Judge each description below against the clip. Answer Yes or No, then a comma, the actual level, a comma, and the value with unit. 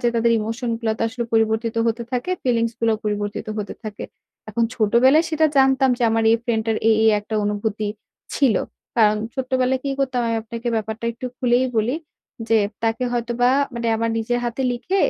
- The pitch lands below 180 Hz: No, high, 230 Hz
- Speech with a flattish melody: Yes, narrow, 2.2 semitones